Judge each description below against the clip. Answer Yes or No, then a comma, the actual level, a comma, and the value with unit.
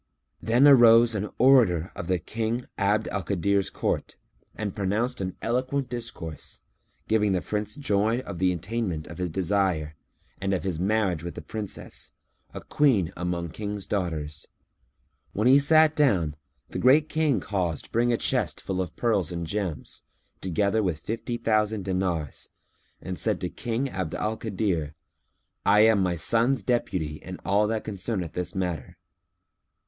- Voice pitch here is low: Yes, low, 100 Hz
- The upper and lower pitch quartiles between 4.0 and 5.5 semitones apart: Yes, average, 4.3 semitones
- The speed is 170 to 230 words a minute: No, average, 155 wpm